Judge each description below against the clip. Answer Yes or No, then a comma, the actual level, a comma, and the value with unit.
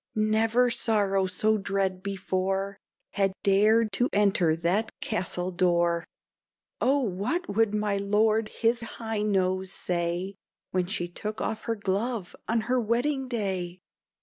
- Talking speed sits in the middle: No, slow, 130 wpm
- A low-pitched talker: No, high, 200 Hz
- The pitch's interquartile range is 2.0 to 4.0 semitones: Yes, average, 3.0 semitones